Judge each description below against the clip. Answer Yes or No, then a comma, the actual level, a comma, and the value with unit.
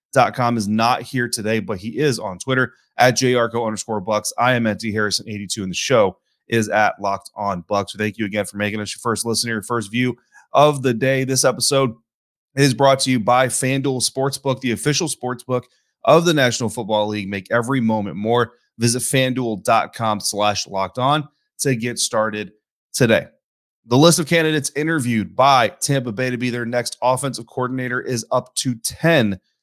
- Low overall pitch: Yes, low, 120 Hz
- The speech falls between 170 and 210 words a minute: Yes, average, 185 wpm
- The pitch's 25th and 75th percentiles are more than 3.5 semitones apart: No, average, 3.2 semitones